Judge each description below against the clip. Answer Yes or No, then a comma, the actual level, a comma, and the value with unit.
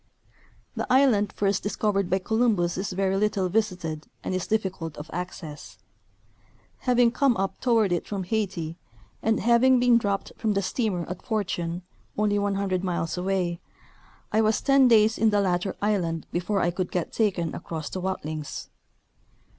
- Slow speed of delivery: No, average, 155 wpm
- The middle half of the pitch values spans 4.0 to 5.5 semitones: No, average, 3.6 semitones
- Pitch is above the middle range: Yes, high, 195 Hz